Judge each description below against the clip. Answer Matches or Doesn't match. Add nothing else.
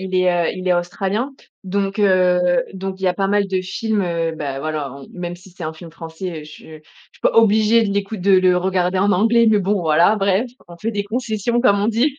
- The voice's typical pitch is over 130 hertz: Matches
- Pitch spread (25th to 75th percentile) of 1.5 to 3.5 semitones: Matches